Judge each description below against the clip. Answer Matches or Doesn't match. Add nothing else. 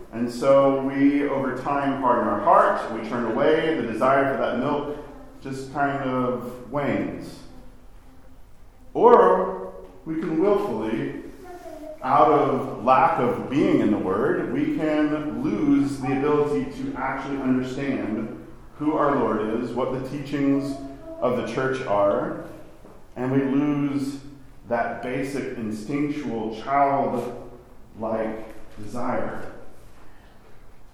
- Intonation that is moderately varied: Matches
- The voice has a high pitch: Doesn't match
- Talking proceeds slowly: Matches